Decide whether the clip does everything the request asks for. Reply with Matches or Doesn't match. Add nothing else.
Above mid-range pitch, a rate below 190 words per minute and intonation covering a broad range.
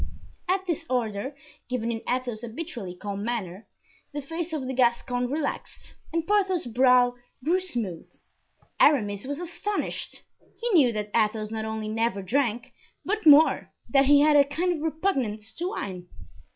Matches